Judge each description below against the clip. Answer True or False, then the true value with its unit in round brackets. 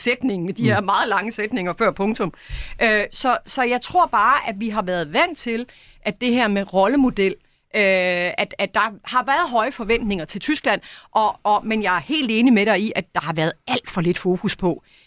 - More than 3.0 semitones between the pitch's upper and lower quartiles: True (4.0 semitones)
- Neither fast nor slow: True (205 wpm)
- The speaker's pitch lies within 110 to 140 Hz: False (210 Hz)